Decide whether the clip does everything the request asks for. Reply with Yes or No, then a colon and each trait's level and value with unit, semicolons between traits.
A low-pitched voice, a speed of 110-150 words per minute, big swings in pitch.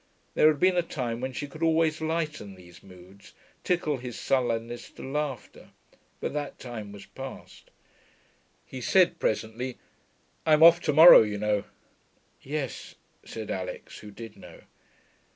Yes: low, 130 Hz; average, 145 wpm; wide, 6.3 semitones